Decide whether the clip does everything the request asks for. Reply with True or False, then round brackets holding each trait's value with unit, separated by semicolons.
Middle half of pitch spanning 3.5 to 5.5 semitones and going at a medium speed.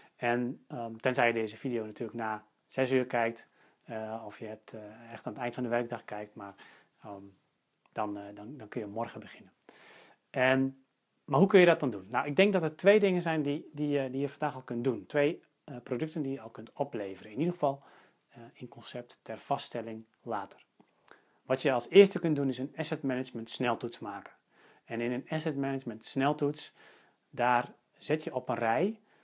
False (4.2 semitones; 205 wpm)